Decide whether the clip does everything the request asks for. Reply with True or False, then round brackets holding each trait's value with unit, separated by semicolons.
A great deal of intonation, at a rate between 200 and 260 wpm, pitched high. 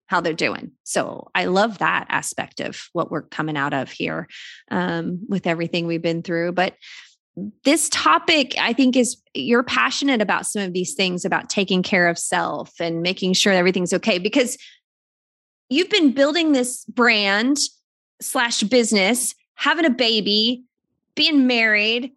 False (6.0 semitones; 155 wpm; 225 Hz)